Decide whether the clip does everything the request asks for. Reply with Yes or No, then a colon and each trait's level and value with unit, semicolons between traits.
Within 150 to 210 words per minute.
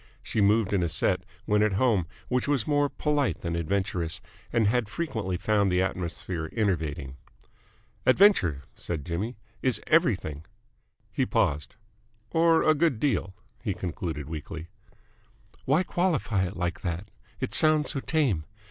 No: average, 140 wpm